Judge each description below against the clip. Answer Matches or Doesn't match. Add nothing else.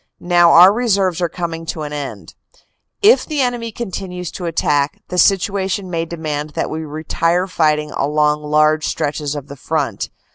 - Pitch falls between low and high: Matches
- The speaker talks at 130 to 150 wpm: Doesn't match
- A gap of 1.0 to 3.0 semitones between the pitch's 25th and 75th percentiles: Doesn't match